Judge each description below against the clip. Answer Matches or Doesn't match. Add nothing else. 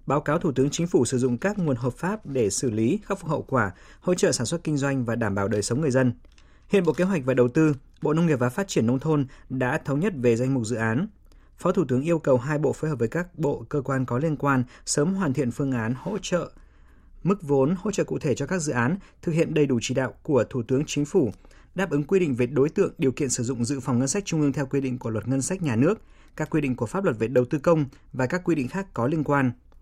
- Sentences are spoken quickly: Matches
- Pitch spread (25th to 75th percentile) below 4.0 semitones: Doesn't match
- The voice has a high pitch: Doesn't match